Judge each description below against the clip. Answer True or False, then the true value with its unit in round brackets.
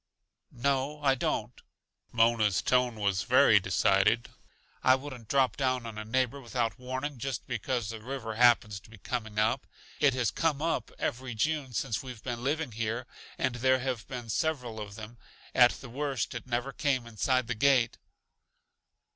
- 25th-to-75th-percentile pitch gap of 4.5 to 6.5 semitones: False (2.8 semitones)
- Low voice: True (125 Hz)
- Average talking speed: True (165 wpm)